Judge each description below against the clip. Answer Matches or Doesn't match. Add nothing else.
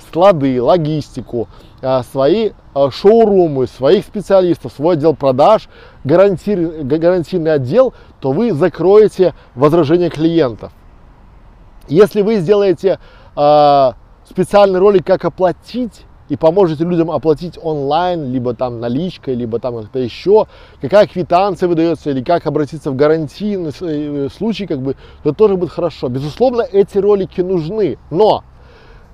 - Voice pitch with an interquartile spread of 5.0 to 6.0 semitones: Matches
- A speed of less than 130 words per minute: Matches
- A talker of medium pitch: Matches